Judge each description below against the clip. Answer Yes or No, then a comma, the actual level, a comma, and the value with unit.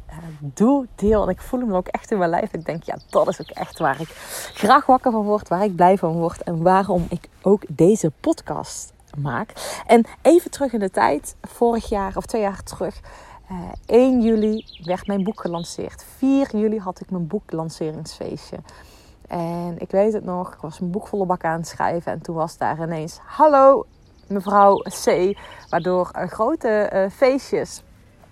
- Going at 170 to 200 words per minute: Yes, average, 190 wpm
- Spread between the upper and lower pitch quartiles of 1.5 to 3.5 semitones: No, average, 4.4 semitones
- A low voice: No, high, 195 Hz